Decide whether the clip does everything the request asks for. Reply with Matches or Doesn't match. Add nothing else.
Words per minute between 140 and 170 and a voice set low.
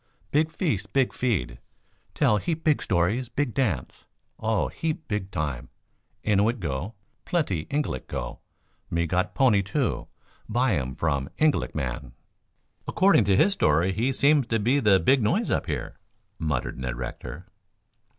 Matches